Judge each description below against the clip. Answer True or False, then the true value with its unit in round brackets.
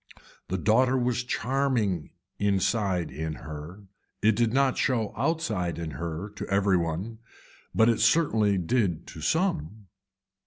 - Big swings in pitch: True (6.0 semitones)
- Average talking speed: False (125 wpm)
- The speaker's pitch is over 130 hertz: False (105 Hz)